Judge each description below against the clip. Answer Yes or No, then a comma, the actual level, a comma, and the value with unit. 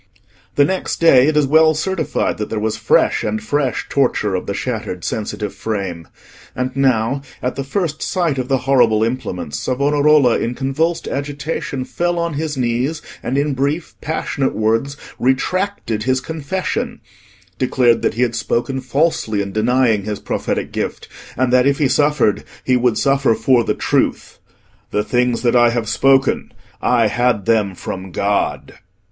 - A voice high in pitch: No, low, 130 Hz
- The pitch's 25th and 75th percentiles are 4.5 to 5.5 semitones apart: No, average, 4.1 semitones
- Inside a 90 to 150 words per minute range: No, average, 160 wpm